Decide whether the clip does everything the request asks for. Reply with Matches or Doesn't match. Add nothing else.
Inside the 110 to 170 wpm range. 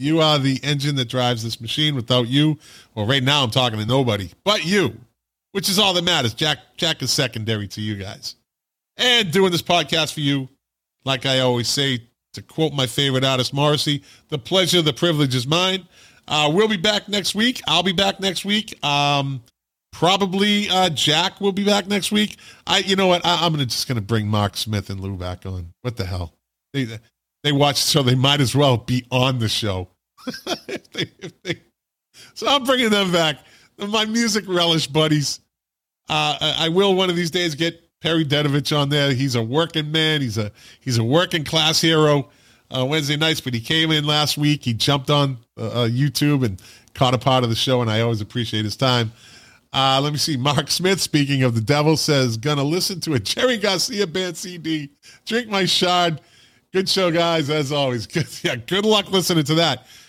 Doesn't match